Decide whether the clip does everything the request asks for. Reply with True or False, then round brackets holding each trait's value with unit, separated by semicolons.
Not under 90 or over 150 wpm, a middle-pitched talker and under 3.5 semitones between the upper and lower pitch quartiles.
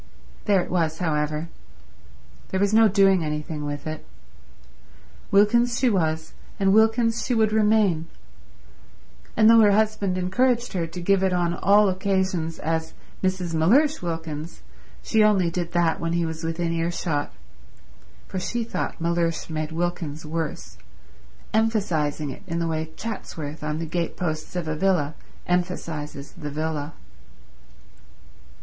False (140 wpm; 175 Hz; 4.0 semitones)